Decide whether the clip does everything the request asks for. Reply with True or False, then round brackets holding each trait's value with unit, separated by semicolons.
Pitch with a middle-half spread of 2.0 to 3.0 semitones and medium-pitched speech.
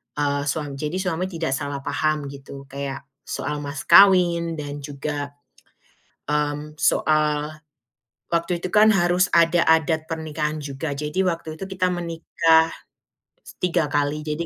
True (2.6 semitones; 155 Hz)